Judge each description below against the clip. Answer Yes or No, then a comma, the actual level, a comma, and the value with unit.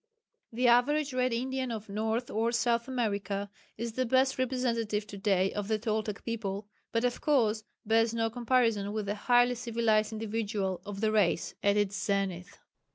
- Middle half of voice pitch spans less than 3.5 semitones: Yes, average, 2.9 semitones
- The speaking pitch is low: No, high, 225 Hz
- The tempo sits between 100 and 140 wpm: No, average, 165 wpm